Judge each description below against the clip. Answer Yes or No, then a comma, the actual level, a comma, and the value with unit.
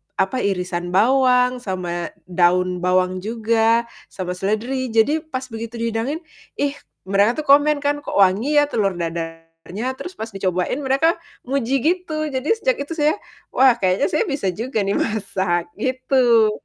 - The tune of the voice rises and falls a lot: Yes, wide, 6.5 semitones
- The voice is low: No, high, 230 Hz